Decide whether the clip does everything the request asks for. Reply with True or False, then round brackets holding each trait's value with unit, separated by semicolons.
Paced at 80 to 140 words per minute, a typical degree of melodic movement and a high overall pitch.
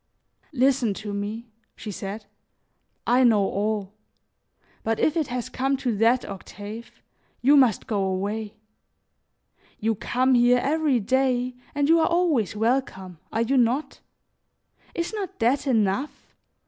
True (135 wpm; 4.2 semitones; 240 Hz)